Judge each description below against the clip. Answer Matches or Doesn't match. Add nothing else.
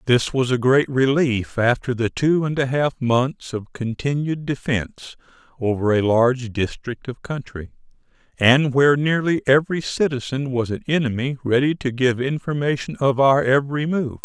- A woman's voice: Doesn't match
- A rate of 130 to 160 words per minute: Matches